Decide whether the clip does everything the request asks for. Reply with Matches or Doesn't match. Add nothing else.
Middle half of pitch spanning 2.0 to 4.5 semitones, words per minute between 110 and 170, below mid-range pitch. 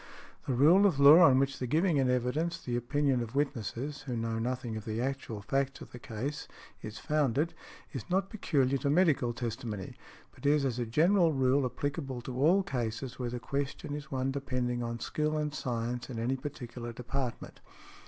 Doesn't match